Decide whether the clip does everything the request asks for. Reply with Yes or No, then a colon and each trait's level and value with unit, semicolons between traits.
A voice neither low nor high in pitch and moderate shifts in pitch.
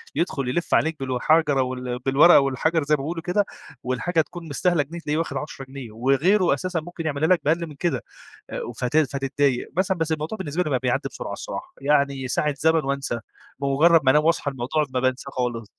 Yes: medium, 145 Hz; average, 3.7 semitones